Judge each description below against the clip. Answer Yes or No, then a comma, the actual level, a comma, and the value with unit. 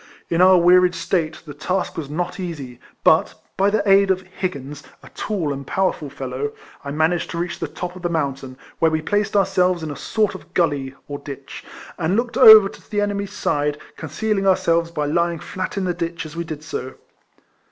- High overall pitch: No, medium, 170 Hz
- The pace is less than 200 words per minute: No, fast, 205 wpm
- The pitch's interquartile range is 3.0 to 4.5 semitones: Yes, average, 4.2 semitones